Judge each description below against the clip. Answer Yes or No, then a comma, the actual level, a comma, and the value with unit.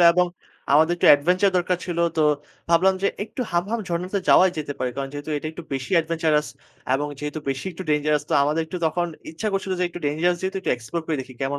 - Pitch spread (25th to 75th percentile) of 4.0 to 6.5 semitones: No, average, 3.5 semitones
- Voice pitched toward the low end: No, medium, 165 Hz